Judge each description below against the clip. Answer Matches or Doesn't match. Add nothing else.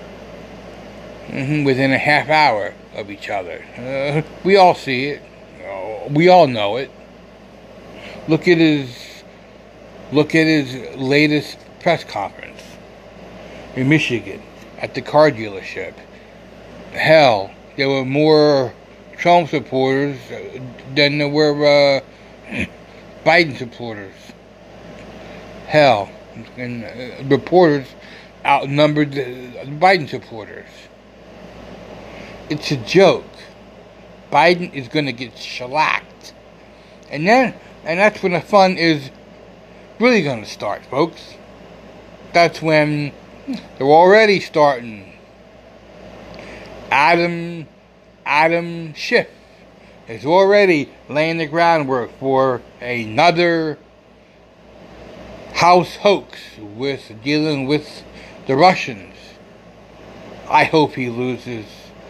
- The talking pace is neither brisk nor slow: Doesn't match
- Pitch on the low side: Doesn't match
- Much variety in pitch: Matches